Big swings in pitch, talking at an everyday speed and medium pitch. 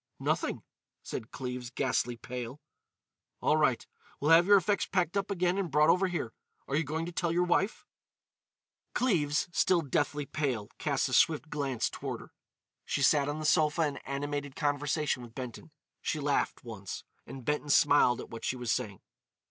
No: average, 4.4 semitones; average, 170 wpm; medium, 145 Hz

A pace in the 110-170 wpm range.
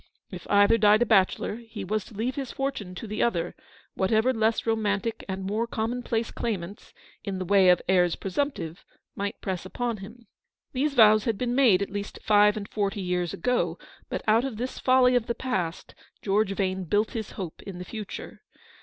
No: average, 190 wpm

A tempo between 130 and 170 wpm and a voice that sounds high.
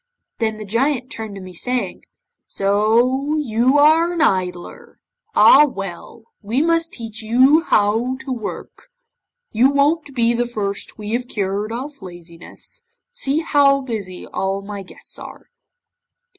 Yes: slow, 135 wpm; high, 235 Hz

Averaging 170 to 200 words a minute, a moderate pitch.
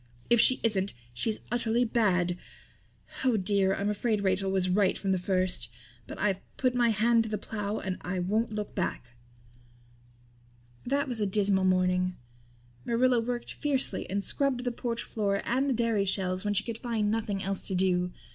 No: average, 175 wpm; high, 205 Hz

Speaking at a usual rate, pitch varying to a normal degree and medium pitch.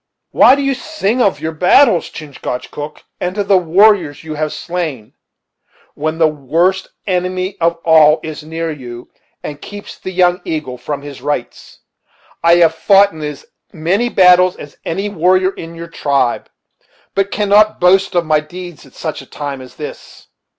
Yes: average, 165 wpm; average, 3.7 semitones; medium, 165 Hz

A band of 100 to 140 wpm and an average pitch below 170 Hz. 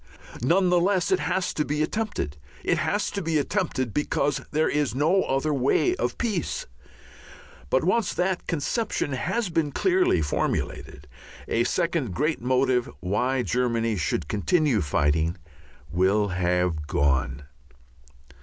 Yes: slow, 135 wpm; medium, 140 Hz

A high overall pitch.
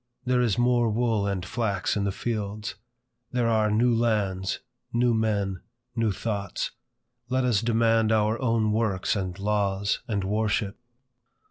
No: low, 110 Hz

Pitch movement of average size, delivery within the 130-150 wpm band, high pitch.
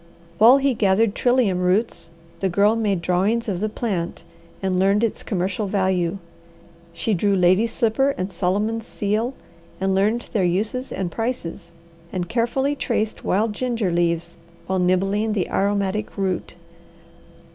Yes: average, 3.5 semitones; average, 140 wpm; high, 200 Hz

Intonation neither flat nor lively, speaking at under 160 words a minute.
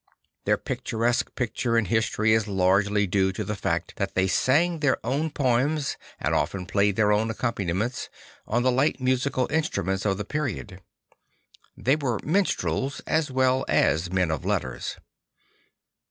Yes: average, 5.0 semitones; average, 150 wpm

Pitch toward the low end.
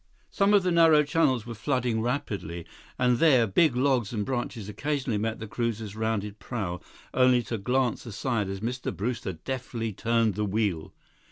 Yes: low, 115 Hz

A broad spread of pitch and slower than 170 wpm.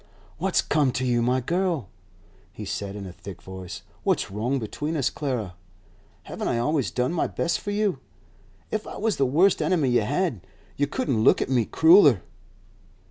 No: wide, 7.3 semitones; average, 180 wpm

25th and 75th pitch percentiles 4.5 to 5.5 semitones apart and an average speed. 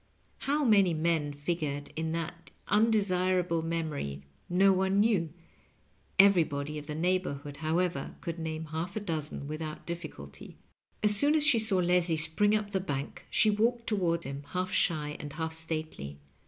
No: average, 4.0 semitones; average, 155 wpm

